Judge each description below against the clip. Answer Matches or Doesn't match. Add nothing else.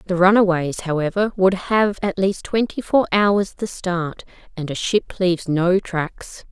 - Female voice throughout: Matches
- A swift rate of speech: Doesn't match